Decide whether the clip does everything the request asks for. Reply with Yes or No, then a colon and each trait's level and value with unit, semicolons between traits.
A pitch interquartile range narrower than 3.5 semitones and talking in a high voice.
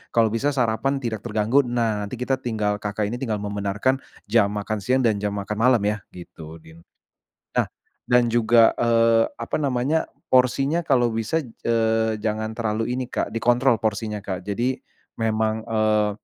No: narrow, 2.6 semitones; low, 115 Hz